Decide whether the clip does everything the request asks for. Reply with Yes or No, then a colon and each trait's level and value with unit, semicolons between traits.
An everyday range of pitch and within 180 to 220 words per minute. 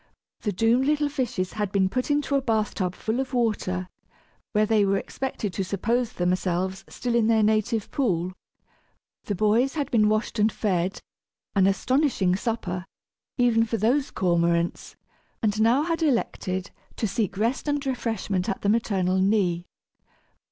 No: average, 4.5 semitones; average, 155 wpm